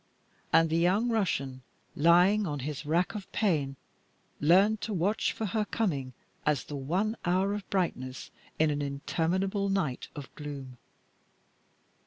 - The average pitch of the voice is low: No, medium, 170 Hz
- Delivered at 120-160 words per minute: Yes, average, 140 wpm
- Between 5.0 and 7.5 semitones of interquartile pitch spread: Yes, wide, 5.5 semitones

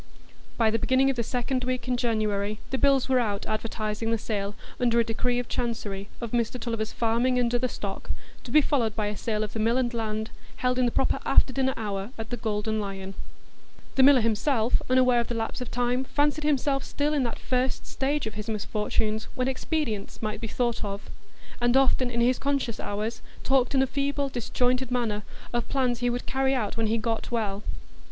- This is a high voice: Yes, high, 240 Hz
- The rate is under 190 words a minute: No, fast, 205 wpm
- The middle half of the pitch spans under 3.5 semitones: Yes, average, 2.9 semitones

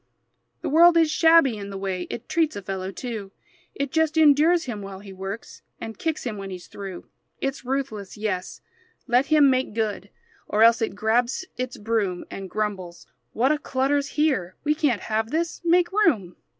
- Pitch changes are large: Yes, wide, 7.0 semitones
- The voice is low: No, high, 235 Hz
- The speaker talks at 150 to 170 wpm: No, average, 180 wpm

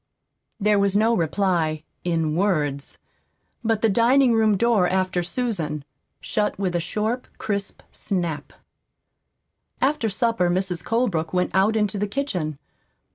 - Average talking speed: No, slow, 130 wpm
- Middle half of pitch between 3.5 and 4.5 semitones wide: Yes, average, 4.2 semitones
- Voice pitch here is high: Yes, high, 195 Hz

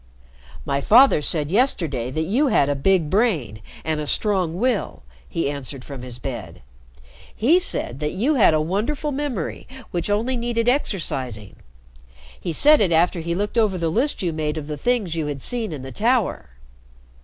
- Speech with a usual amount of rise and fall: No, wide, 8.2 semitones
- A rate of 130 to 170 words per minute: No, average, 180 wpm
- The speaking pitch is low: No, medium, 170 Hz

